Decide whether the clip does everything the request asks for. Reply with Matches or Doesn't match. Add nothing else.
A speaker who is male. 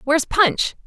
Doesn't match